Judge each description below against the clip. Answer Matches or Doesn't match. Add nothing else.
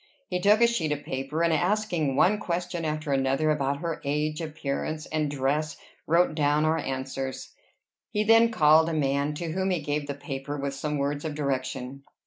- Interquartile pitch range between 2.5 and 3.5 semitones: Matches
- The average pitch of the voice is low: Doesn't match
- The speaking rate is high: Doesn't match